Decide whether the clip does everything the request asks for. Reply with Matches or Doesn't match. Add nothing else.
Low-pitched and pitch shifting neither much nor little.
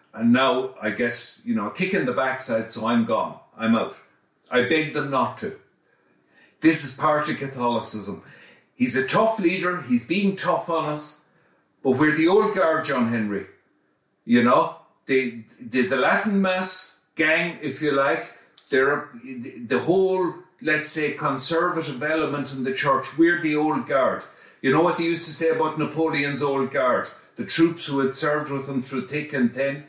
Doesn't match